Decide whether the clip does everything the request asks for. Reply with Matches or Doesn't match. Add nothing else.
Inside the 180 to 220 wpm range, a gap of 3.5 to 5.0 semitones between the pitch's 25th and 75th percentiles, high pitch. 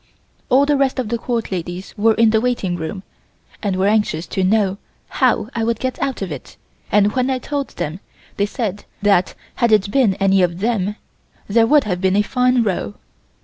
Matches